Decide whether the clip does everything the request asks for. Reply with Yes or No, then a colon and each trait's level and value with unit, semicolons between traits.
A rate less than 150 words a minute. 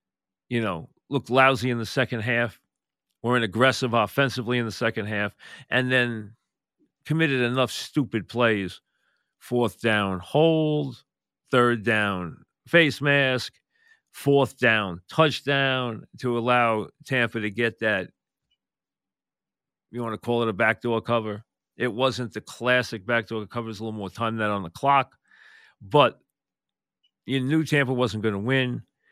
Yes: average, 140 wpm